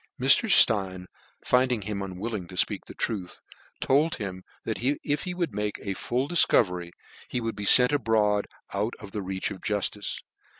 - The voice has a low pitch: Yes, low, 105 Hz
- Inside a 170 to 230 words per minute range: Yes, average, 180 wpm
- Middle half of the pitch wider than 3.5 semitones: Yes, average, 4.4 semitones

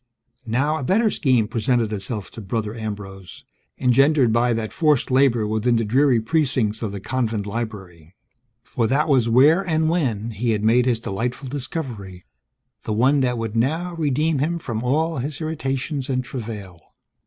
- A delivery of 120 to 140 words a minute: No, average, 165 wpm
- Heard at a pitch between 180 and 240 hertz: No, low, 125 Hz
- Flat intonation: No, average, 4.5 semitones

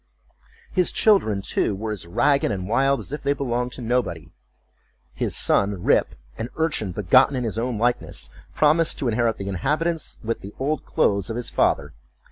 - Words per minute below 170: No, average, 175 wpm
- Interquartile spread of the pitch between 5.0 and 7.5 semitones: Yes, wide, 5.4 semitones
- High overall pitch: No, low, 120 Hz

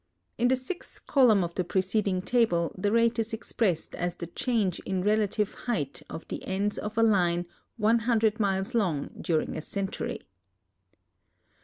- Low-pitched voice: No, high, 205 Hz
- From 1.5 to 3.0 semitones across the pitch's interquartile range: No, average, 3.8 semitones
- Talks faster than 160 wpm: No, average, 155 wpm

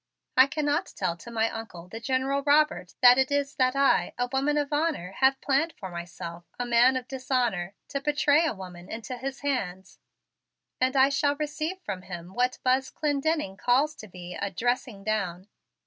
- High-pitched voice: Yes, very high, 255 Hz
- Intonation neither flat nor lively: No, wide, 6.3 semitones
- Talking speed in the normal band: Yes, average, 185 wpm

